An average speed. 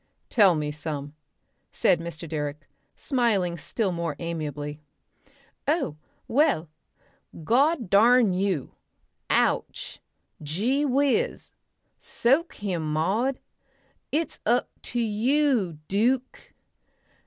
No: slow, 90 wpm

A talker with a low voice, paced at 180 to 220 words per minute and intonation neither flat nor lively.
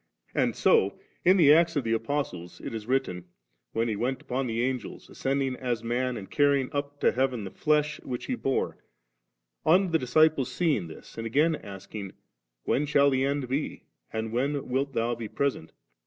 Yes: low, 130 Hz; average, 185 wpm; average, 4.0 semitones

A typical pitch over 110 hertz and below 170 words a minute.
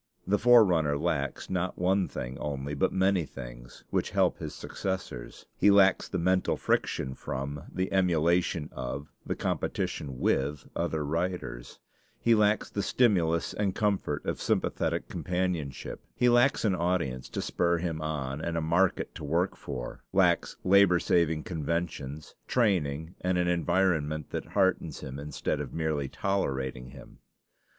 No: very low, 85 Hz; average, 145 wpm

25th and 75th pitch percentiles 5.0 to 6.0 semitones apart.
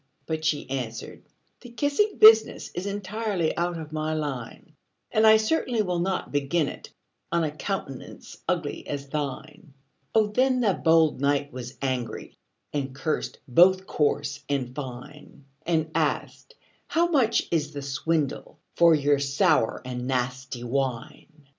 Yes: wide, 5.4 semitones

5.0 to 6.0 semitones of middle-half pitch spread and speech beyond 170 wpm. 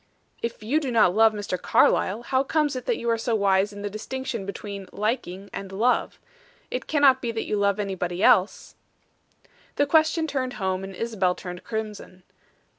No: average, 4.6 semitones; average, 180 wpm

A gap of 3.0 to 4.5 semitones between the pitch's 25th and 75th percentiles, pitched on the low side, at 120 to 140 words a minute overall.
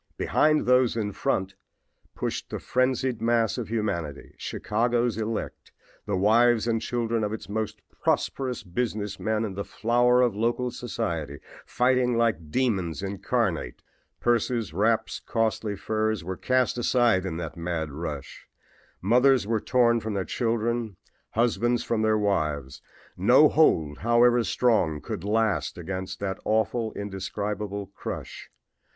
Yes: average, 3.7 semitones; low, 110 Hz; slow, 135 wpm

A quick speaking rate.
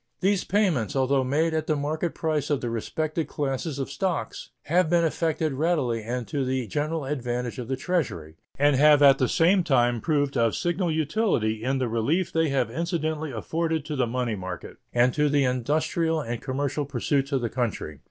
No: average, 190 wpm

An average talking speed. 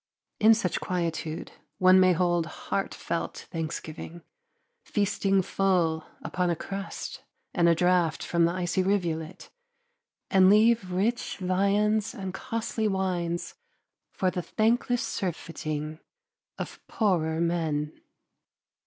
No: slow, 110 wpm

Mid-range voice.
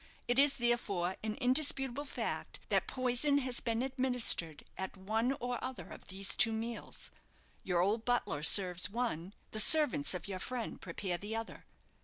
No: high, 230 Hz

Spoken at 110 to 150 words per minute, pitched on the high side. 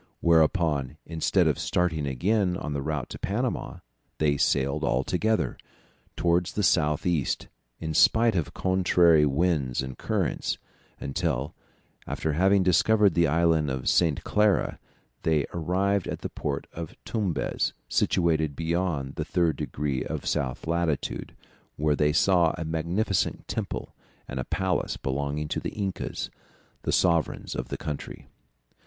No: average, 140 wpm; very low, 80 Hz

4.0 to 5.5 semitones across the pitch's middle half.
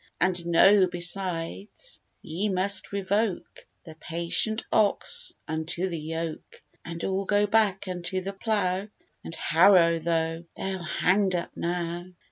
No: average, 2.9 semitones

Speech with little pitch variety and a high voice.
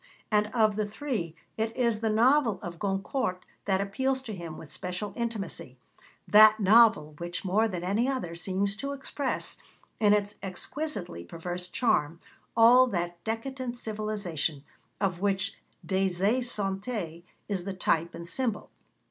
No: average, 4.2 semitones; high, 205 Hz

